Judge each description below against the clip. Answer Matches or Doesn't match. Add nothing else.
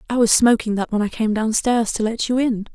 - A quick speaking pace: Matches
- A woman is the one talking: Matches